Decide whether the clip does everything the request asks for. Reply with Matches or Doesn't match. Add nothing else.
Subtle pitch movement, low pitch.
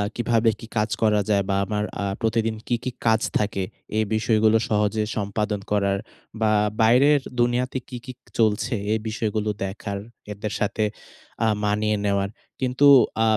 Matches